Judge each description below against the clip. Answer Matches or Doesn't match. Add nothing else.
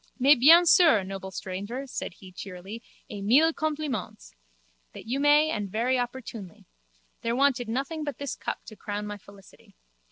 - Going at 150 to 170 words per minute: Matches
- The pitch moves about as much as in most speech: Doesn't match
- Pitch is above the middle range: Matches